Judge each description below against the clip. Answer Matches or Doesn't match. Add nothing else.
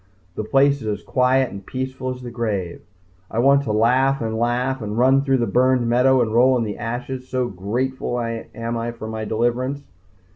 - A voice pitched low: Matches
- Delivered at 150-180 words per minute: Doesn't match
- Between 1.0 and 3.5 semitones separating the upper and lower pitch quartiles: Matches